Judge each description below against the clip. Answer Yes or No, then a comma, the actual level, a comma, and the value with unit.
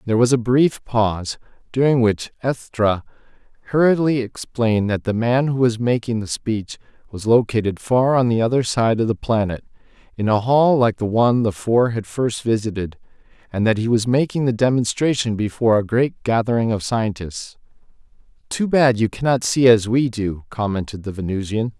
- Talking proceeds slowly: No, average, 175 wpm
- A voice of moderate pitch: No, low, 115 Hz